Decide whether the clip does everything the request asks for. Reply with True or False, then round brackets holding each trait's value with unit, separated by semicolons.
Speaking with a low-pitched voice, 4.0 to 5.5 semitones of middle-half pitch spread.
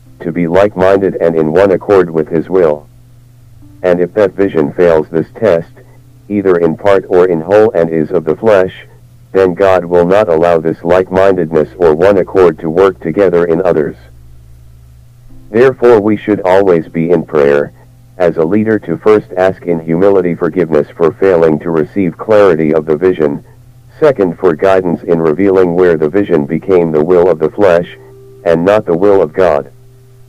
True (95 Hz; 4.6 semitones)